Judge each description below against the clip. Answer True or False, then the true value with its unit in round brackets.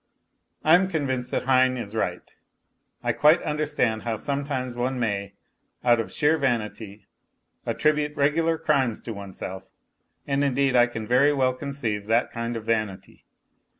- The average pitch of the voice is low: True (125 Hz)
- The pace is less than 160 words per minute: True (150 wpm)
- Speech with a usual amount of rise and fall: True (4.1 semitones)